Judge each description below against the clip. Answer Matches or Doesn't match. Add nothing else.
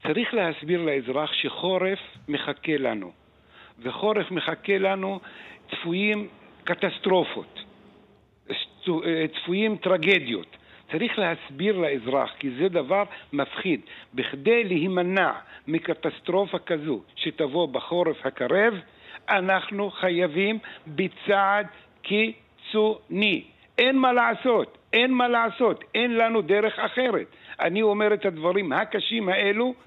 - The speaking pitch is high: Matches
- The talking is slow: Matches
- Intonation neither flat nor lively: Matches